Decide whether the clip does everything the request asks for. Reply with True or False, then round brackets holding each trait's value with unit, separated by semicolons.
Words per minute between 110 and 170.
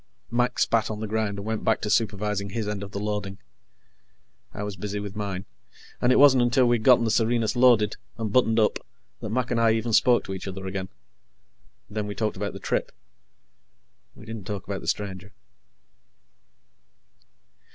False (185 wpm)